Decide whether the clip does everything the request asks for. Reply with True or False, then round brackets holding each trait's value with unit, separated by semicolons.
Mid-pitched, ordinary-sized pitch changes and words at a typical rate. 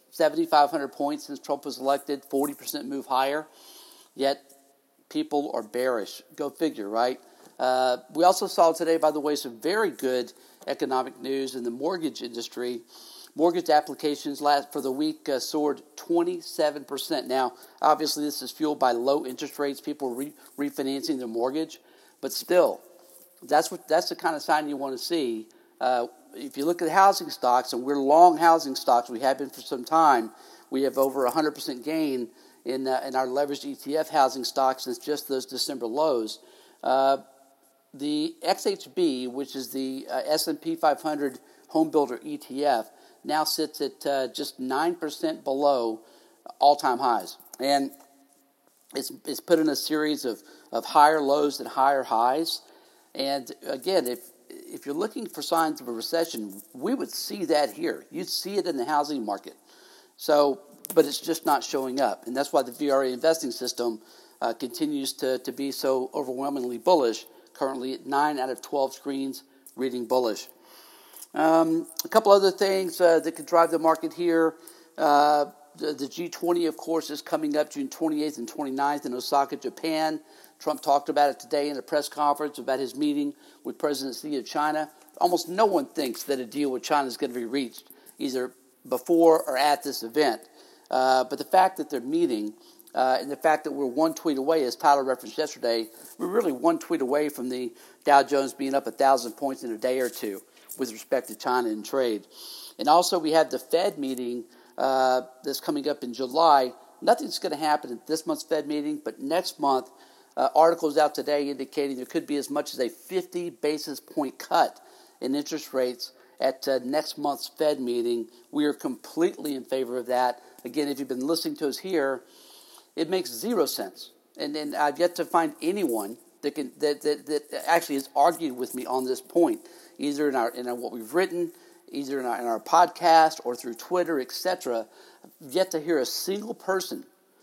True (145 Hz; 3.4 semitones; 185 wpm)